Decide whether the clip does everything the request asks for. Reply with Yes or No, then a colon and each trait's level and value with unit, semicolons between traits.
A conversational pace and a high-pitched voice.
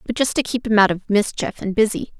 No: fast, 275 wpm; high, 215 Hz